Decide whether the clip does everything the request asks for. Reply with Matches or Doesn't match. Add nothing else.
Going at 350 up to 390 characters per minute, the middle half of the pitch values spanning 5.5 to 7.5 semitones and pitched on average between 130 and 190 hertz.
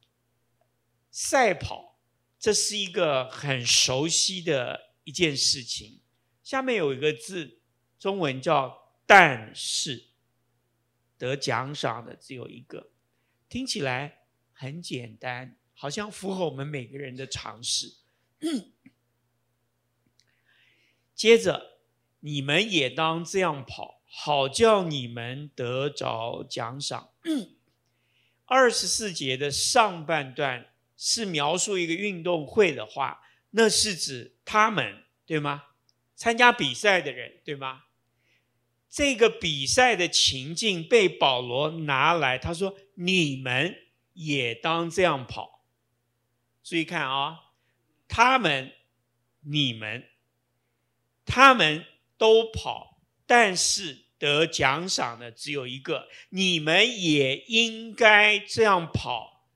Doesn't match